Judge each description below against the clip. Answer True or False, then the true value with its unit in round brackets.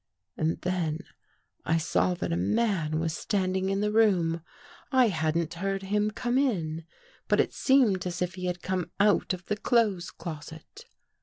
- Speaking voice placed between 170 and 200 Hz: True (185 Hz)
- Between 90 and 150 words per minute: False (165 wpm)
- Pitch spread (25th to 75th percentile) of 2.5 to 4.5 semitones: True (4.1 semitones)